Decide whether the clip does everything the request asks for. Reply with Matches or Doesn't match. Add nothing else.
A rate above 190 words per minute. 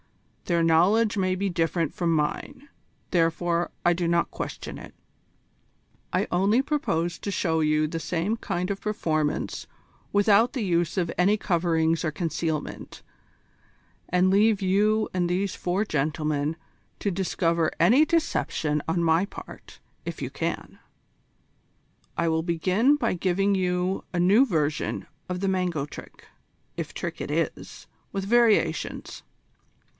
Doesn't match